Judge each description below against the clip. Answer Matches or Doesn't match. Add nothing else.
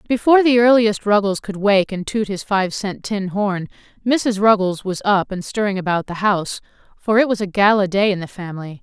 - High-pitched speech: Matches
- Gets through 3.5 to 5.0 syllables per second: Doesn't match